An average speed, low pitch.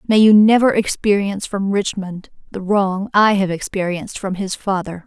No: average, 165 wpm; high, 195 Hz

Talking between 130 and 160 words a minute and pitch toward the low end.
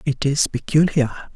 No: slow, 135 wpm; medium, 145 Hz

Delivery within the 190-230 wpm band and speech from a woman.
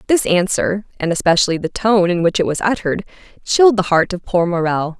Yes: fast, 205 wpm; female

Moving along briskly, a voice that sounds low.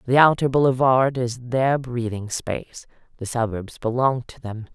No: average, 150 wpm; low, 125 Hz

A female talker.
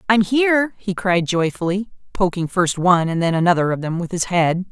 Yes: female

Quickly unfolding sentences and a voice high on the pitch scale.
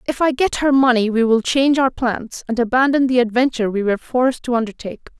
Yes: fast, 220 wpm; high, 245 Hz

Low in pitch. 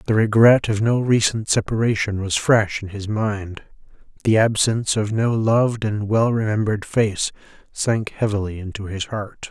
Yes: low, 105 Hz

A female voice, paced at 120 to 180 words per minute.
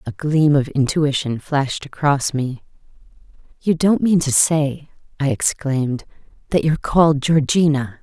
Yes: female; slow, 135 wpm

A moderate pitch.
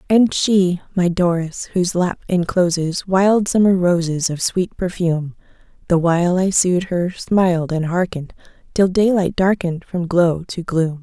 Yes: medium, 180 Hz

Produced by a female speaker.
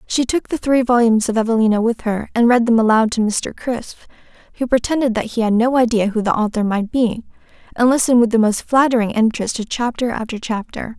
Yes: female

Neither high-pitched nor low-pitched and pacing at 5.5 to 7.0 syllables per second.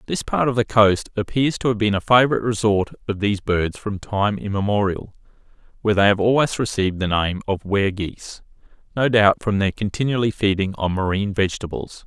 No: low, 105 Hz; 5.8 syllables/s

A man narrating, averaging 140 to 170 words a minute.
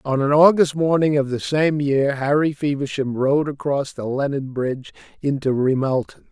Yes: male; average, 160 wpm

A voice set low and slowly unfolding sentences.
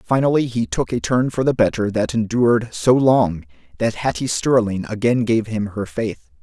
No: low, 115 Hz; average, 185 wpm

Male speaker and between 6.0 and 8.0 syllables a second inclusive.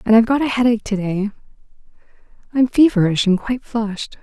No: female; 6.6 syllables/s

